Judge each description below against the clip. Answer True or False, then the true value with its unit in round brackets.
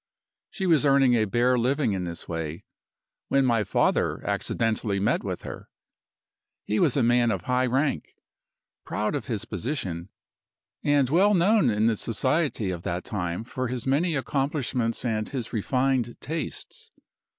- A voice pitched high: False (125 Hz)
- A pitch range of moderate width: True (4.3 semitones)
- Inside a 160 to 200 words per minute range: False (150 wpm)